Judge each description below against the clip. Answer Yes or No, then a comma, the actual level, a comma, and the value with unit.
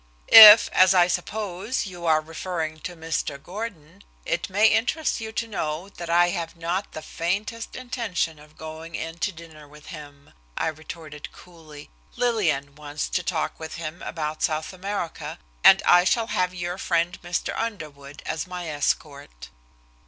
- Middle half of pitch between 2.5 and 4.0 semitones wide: Yes, average, 3.5 semitones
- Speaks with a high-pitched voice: No, medium, 170 Hz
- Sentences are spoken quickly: No, average, 160 wpm